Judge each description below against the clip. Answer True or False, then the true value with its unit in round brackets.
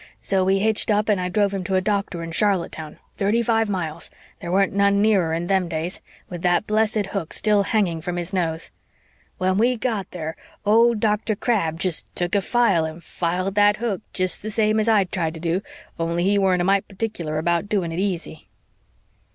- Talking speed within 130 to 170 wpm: False (200 wpm)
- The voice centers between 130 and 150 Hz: False (190 Hz)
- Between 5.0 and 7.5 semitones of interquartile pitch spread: False (3.4 semitones)